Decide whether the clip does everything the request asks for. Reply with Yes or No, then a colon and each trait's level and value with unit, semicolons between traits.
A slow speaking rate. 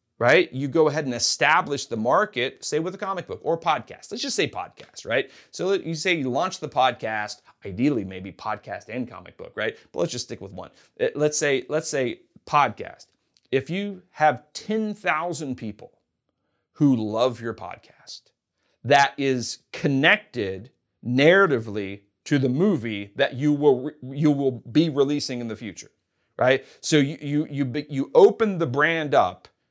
No: average, 165 wpm